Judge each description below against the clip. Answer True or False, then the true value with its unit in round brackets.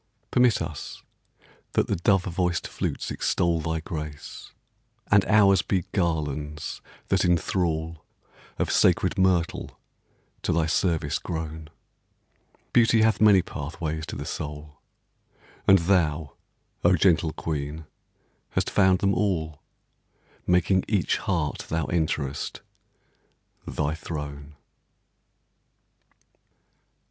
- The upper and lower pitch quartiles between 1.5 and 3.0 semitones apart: False (3.4 semitones)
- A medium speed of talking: False (100 wpm)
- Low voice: True (85 Hz)